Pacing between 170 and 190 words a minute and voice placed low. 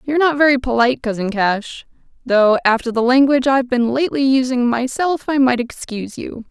No: average, 175 wpm; very high, 255 Hz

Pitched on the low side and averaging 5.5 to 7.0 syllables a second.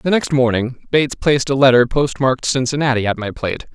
Yes: low, 130 Hz; 6.1 syllables/s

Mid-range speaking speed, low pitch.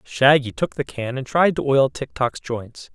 No: fast, 225 wpm; low, 130 Hz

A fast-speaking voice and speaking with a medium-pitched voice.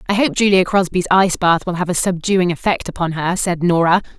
Yes: fast, 215 wpm; medium, 180 Hz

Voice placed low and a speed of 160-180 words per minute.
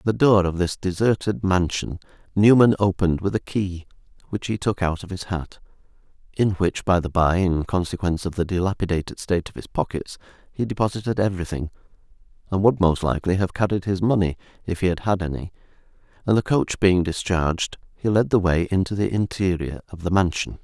Yes: very low, 95 Hz; average, 175 wpm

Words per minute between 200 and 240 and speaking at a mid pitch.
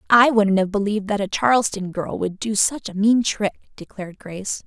No: fast, 205 wpm; high, 205 Hz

